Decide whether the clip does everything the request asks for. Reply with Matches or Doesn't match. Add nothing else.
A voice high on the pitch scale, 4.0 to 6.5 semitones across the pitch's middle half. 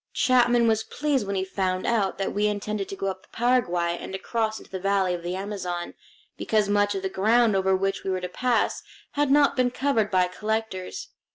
Doesn't match